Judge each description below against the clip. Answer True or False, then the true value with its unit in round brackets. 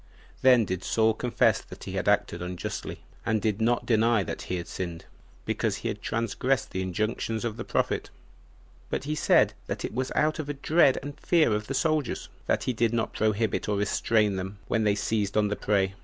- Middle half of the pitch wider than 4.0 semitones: False (3.4 semitones)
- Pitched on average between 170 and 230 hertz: False (110 Hz)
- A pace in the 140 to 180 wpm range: False (205 wpm)